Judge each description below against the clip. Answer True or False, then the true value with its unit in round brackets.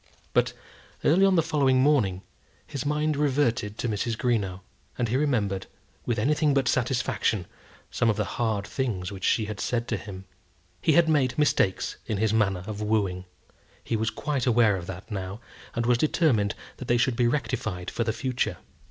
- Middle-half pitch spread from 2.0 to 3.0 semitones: False (4.9 semitones)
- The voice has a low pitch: True (115 Hz)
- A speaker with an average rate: True (180 wpm)